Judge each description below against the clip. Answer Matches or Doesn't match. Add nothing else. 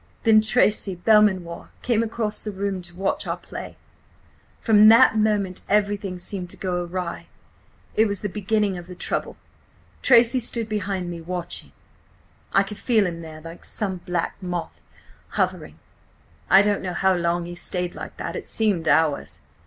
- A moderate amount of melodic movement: Matches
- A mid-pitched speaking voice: Doesn't match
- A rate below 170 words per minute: Matches